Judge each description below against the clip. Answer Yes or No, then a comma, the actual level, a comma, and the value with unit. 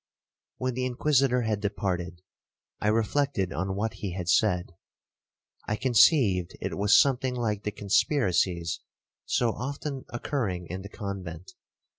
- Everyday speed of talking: No, slow, 130 wpm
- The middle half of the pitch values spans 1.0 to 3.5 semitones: No, average, 5.2 semitones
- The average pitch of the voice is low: Yes, low, 105 Hz